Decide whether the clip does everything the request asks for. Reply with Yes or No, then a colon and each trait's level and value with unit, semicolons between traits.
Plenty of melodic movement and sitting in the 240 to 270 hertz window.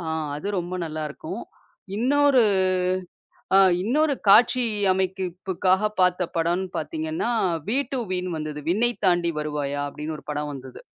No: wide, 7.4 semitones; medium, 185 Hz